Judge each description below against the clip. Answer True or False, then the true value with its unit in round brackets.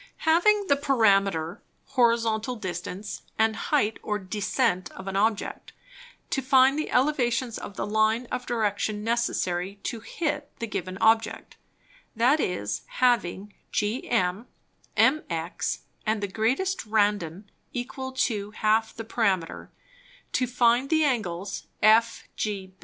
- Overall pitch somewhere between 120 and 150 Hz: False (220 Hz)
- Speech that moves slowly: True (120 wpm)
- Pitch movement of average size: True (4.1 semitones)